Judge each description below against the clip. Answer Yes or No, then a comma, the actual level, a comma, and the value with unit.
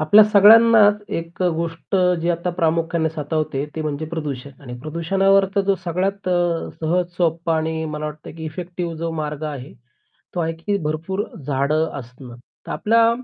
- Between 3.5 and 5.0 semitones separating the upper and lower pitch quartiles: No, average, 3.0 semitones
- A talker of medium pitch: Yes, medium, 165 Hz